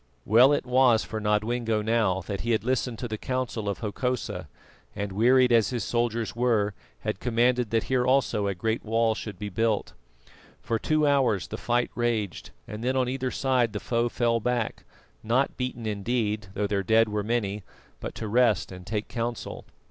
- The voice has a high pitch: No, low, 115 Hz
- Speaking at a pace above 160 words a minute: Yes, average, 185 wpm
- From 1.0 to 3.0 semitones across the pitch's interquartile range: Yes, average, 2.7 semitones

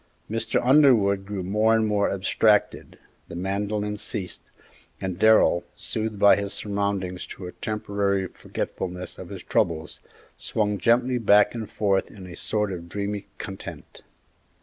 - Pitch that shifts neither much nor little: No, narrow, 2.1 semitones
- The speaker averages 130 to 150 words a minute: Yes, average, 140 wpm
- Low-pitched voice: Yes, low, 100 Hz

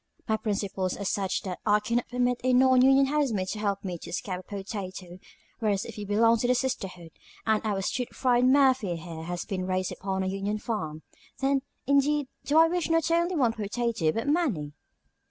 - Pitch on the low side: No, high, 215 Hz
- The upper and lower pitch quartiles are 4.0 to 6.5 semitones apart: Yes, wide, 5.4 semitones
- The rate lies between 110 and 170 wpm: No, average, 195 wpm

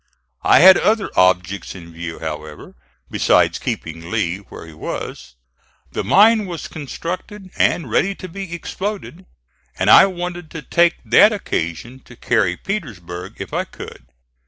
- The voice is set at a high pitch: No, medium, 145 Hz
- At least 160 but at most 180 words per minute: No, average, 145 wpm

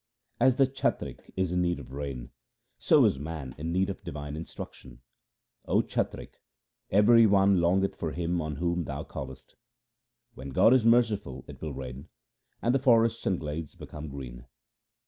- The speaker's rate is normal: Yes, average, 165 wpm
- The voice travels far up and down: Yes, wide, 6.2 semitones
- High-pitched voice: No, very low, 85 Hz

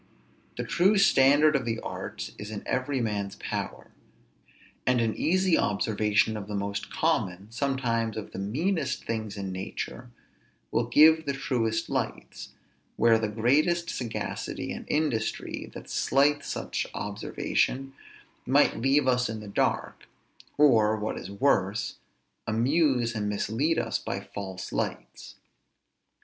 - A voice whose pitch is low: Yes, low, 115 Hz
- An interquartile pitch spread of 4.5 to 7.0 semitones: Yes, average, 4.9 semitones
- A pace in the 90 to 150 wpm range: Yes, slow, 135 wpm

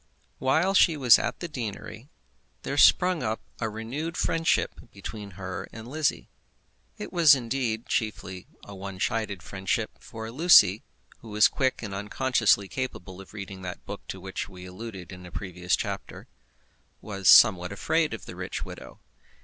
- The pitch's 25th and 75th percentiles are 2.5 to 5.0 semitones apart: No, wide, 5.4 semitones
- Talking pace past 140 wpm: Yes, average, 155 wpm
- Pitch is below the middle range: Yes, low, 110 Hz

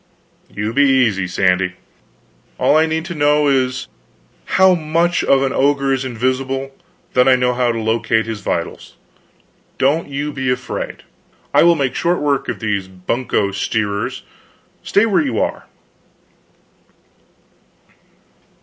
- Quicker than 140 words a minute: No, slow, 135 wpm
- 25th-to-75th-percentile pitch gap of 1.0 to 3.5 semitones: No, average, 4.6 semitones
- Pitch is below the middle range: Yes, low, 130 Hz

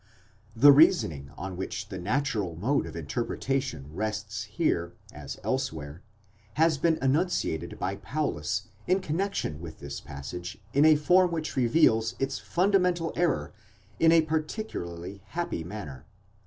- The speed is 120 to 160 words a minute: Yes, slow, 135 wpm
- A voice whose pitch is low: Yes, low, 115 Hz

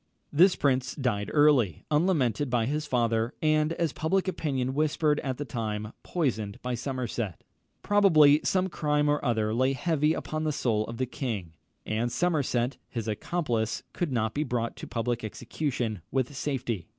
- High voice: No, low, 130 Hz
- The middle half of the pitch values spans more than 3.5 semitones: Yes, average, 4.6 semitones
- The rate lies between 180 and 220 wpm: No, average, 160 wpm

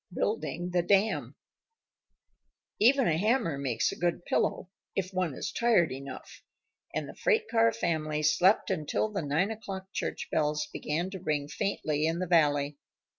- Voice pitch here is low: No, medium, 175 Hz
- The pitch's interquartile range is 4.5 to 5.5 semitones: Yes, average, 4.8 semitones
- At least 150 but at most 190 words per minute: Yes, average, 155 wpm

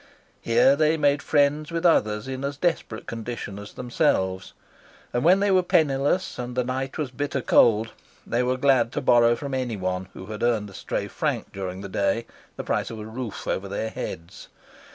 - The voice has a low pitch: Yes, low, 120 Hz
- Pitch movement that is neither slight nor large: Yes, average, 5.0 semitones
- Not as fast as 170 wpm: No, average, 190 wpm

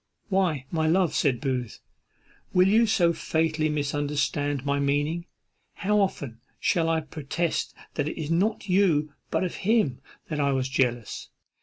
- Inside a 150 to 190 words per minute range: Yes, average, 155 wpm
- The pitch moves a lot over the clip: No, average, 4.2 semitones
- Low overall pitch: No, medium, 155 Hz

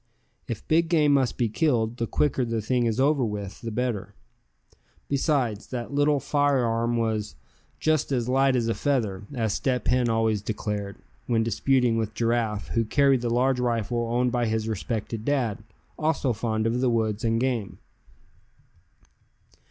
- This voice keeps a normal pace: Yes, average, 160 wpm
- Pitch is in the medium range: No, low, 120 Hz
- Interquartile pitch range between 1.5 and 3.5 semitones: Yes, average, 2.9 semitones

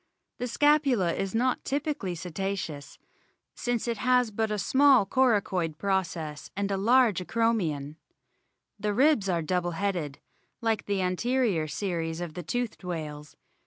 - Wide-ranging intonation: Yes, wide, 5.8 semitones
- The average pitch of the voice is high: Yes, high, 195 Hz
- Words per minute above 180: No, slow, 135 wpm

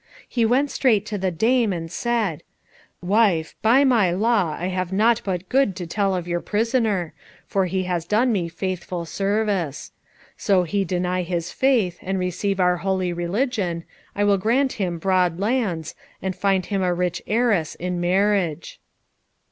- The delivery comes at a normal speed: Yes, average, 165 wpm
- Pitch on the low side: No, high, 190 Hz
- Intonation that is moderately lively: Yes, average, 3.6 semitones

